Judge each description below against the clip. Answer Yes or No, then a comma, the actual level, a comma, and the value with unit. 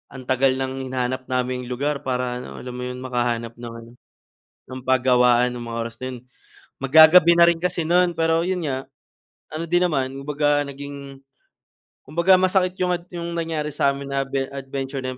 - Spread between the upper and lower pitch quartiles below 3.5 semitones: No, average, 4.3 semitones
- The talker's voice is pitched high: No, low, 135 Hz